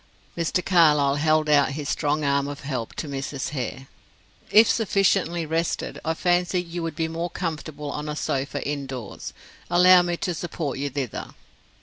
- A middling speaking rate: Yes, average, 160 wpm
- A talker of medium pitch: Yes, medium, 155 Hz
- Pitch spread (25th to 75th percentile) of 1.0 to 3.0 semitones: No, average, 3.5 semitones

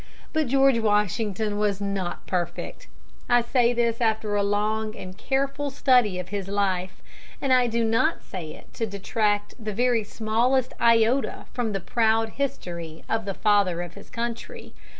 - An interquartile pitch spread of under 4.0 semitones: Yes, average, 3.1 semitones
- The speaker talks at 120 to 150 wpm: No, average, 160 wpm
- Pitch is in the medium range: No, high, 220 Hz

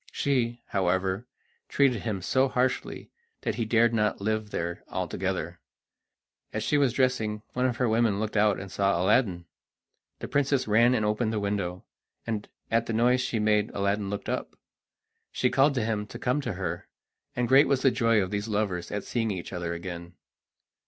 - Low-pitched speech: Yes, low, 110 Hz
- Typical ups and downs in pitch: Yes, average, 3.8 semitones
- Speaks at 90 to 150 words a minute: No, average, 180 wpm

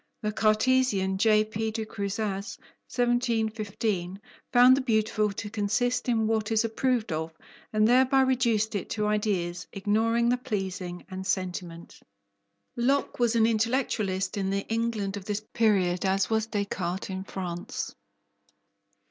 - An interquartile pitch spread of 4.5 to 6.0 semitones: No, average, 3.1 semitones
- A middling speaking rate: No, slow, 130 wpm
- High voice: Yes, high, 215 Hz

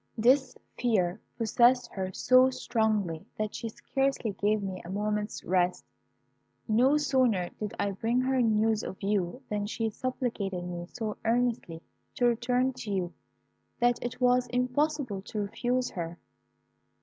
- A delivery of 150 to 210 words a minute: No, average, 140 wpm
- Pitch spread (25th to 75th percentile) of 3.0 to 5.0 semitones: Yes, average, 3.9 semitones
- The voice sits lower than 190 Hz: No, high, 225 Hz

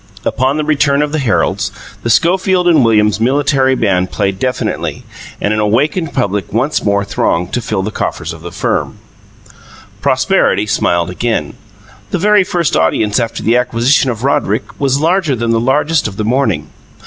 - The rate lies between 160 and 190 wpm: Yes, average, 170 wpm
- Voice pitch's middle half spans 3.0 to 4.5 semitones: No, wide, 5.6 semitones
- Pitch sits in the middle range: No, low, 125 Hz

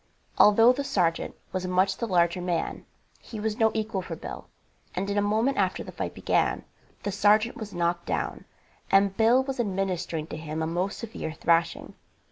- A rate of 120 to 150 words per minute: No, average, 180 wpm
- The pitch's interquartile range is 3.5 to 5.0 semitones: Yes, average, 4.1 semitones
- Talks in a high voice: Yes, high, 195 Hz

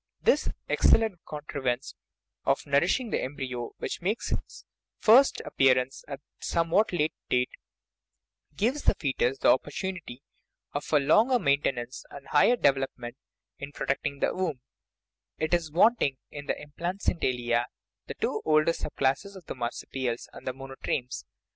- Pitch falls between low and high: Yes, medium, 145 Hz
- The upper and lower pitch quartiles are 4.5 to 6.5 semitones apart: Yes, average, 4.9 semitones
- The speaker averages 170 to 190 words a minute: No, average, 150 wpm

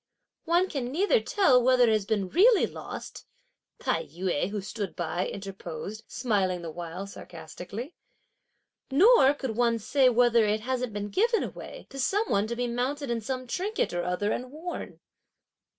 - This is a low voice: No, high, 240 Hz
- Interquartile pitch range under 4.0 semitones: No, wide, 5.6 semitones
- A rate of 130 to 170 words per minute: Yes, average, 165 wpm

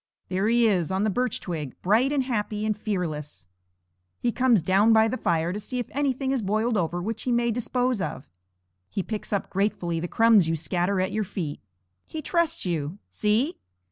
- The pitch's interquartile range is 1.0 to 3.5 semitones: No, average, 4.9 semitones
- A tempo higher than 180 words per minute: Yes, average, 195 wpm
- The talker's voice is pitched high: Yes, high, 210 Hz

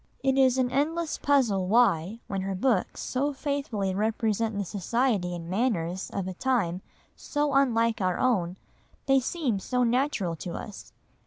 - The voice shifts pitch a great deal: Yes, wide, 5.7 semitones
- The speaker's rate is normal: Yes, average, 155 wpm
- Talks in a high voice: Yes, high, 225 Hz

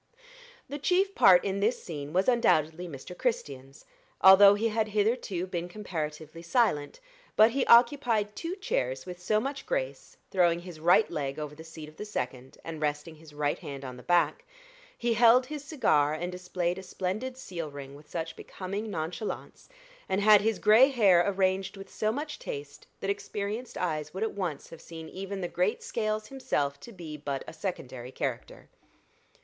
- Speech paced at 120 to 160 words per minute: No, average, 175 wpm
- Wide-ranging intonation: Yes, wide, 5.7 semitones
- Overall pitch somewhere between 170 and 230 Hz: Yes, medium, 185 Hz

